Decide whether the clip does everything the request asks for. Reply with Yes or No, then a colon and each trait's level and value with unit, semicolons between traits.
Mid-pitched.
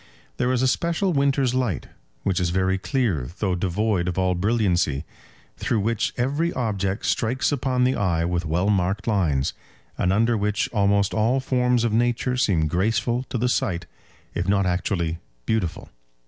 No: low, 105 Hz